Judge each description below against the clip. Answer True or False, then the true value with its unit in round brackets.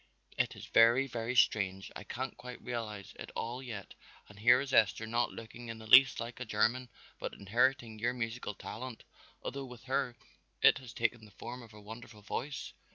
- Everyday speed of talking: True (190 wpm)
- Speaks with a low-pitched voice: True (120 Hz)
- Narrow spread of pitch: True (2.2 semitones)